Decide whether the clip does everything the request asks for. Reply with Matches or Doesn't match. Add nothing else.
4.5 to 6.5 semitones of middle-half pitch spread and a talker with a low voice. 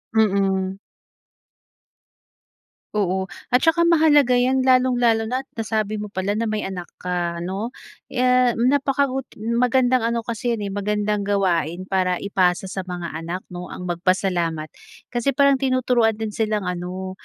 Doesn't match